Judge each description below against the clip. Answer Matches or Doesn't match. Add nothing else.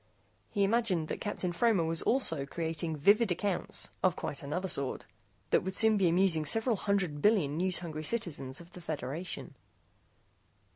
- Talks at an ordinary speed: Matches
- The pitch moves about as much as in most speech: Matches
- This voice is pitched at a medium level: Matches